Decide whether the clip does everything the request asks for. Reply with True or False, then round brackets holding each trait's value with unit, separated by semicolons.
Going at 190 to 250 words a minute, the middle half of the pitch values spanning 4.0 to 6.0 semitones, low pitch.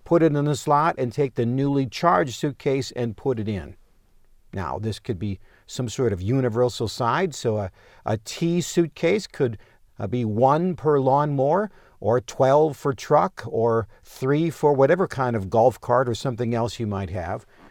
False (175 wpm; 4.6 semitones; 130 Hz)